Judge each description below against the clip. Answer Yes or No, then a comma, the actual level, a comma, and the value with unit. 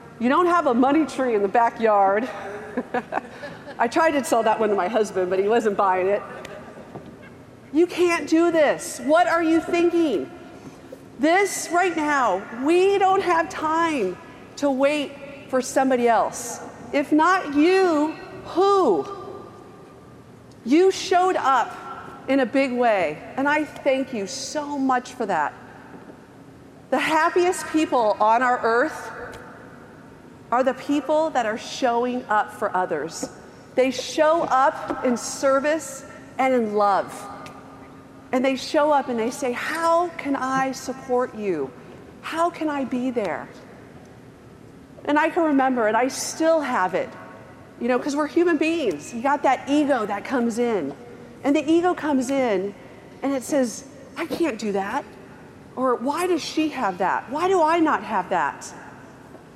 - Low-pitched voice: No, very high, 275 Hz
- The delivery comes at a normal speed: Yes, average, 150 wpm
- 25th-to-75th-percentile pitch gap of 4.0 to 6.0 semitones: Yes, average, 4.9 semitones